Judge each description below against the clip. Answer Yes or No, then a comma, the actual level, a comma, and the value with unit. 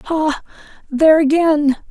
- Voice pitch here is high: Yes, very high, 305 Hz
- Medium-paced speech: No, slow, 95 wpm